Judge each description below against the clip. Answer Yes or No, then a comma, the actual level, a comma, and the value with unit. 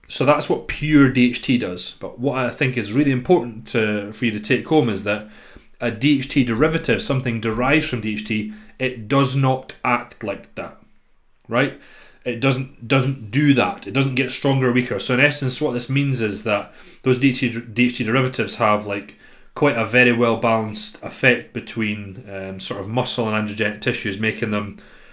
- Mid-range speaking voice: No, low, 125 Hz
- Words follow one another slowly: No, average, 180 wpm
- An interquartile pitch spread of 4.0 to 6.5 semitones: No, average, 3.5 semitones